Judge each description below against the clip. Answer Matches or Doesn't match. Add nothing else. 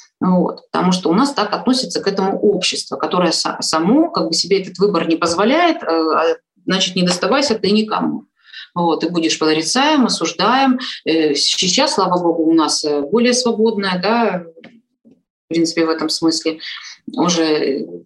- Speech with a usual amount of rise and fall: Doesn't match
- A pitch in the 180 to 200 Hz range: Matches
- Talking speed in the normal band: Matches